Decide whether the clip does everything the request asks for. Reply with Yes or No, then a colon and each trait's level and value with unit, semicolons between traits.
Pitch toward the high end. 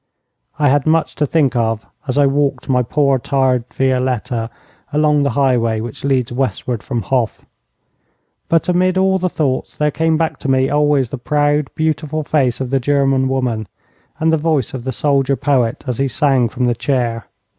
No: low, 135 Hz